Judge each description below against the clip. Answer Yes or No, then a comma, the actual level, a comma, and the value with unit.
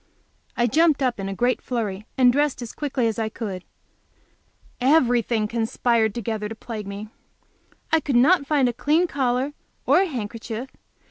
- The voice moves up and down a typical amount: Yes, average, 3.9 semitones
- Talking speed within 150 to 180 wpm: Yes, average, 160 wpm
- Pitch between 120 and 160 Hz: No, high, 240 Hz